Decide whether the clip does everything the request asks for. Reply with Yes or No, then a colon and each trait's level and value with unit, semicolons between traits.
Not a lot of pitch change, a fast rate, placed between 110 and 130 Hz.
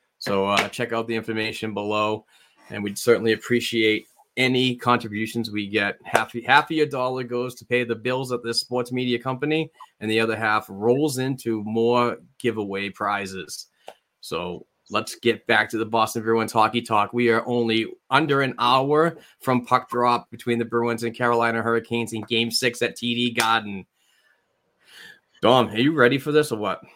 No: narrow, 1.8 semitones; average, 175 wpm; low, 115 Hz